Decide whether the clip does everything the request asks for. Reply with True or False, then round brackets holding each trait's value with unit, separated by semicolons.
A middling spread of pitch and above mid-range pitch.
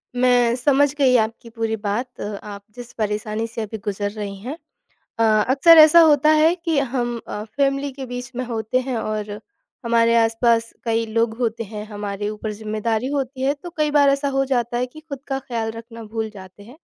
True (3.7 semitones; 235 Hz)